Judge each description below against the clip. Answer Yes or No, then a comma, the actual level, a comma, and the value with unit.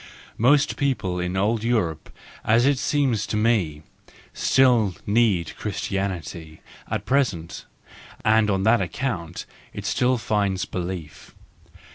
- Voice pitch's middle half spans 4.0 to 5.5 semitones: Yes, average, 4.9 semitones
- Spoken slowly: Yes, slow, 115 wpm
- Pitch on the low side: Yes, low, 105 Hz